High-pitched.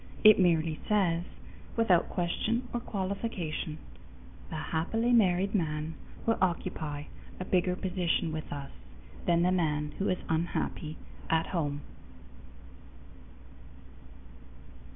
No: medium, 175 Hz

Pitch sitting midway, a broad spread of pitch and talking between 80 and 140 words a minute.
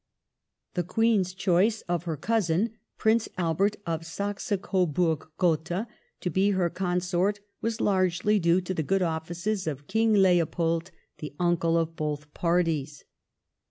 No: medium, 180 Hz; average, 3.1 semitones; slow, 135 wpm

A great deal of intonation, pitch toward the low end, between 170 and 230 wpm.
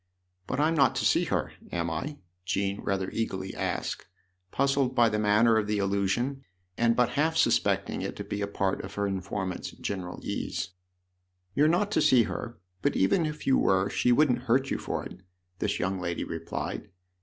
Yes: wide, 5.7 semitones; low, 105 Hz; average, 200 wpm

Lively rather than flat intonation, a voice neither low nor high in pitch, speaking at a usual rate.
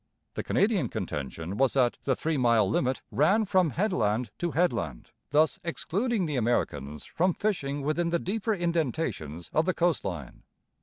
Yes: wide, 7.6 semitones; medium, 150 Hz; average, 155 wpm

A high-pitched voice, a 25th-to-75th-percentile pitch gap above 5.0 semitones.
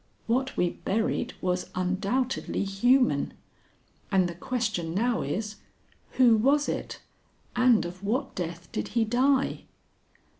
Yes: high, 215 Hz; wide, 5.4 semitones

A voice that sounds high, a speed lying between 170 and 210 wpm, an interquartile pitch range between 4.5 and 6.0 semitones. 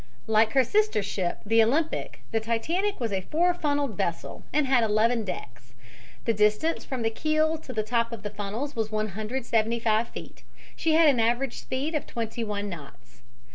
Yes: high, 230 Hz; average, 175 wpm; average, 4.8 semitones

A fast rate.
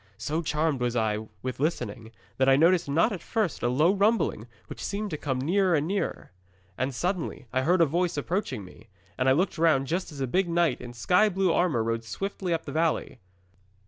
Yes: fast, 210 wpm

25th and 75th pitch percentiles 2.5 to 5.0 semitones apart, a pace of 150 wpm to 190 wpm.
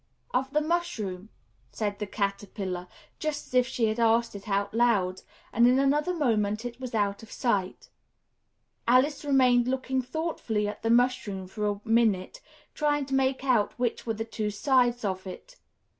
Yes: average, 4.3 semitones; average, 165 wpm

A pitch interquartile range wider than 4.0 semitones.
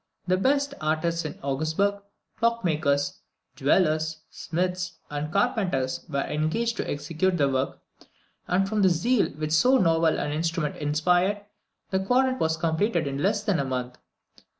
Yes: average, 4.6 semitones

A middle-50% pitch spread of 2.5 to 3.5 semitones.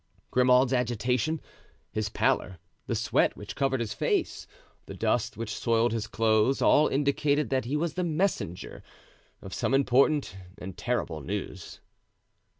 No: average, 4.5 semitones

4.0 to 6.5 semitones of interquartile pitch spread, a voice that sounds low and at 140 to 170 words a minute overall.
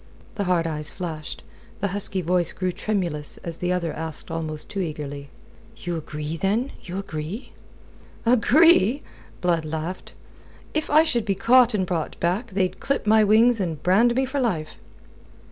No: average, 5.2 semitones; medium, 185 Hz; average, 160 wpm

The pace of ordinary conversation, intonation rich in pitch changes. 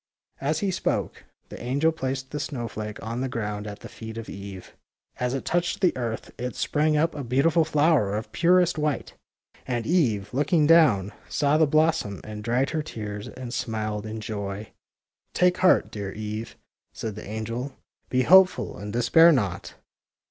Yes: average, 175 wpm; wide, 6.1 semitones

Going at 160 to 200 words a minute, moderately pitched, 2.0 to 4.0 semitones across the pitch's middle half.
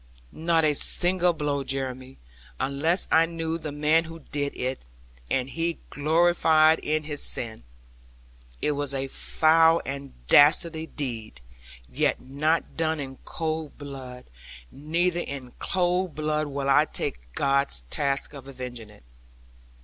No: slow, 135 wpm; medium, 150 Hz; average, 3.2 semitones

